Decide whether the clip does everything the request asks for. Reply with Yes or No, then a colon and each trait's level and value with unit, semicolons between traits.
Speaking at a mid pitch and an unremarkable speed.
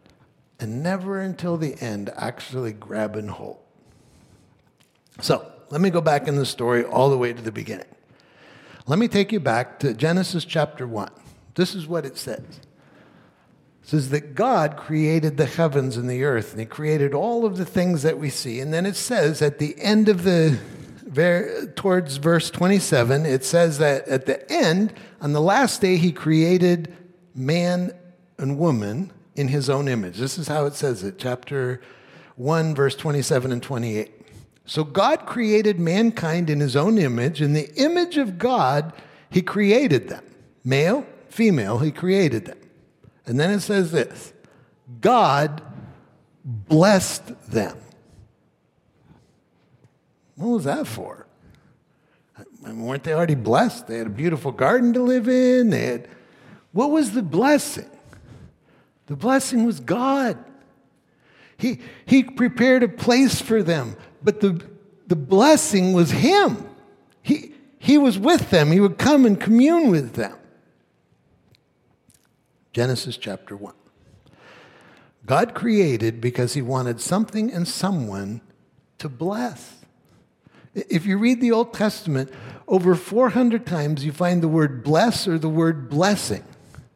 Yes: medium, 165 Hz; average, 145 wpm